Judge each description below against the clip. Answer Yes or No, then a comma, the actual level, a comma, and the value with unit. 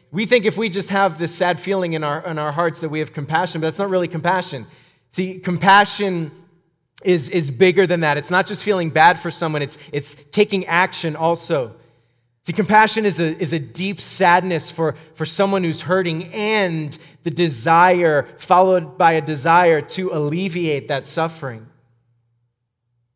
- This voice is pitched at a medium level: Yes, medium, 165 Hz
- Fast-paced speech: No, average, 170 wpm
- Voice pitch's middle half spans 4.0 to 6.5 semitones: No, average, 3.5 semitones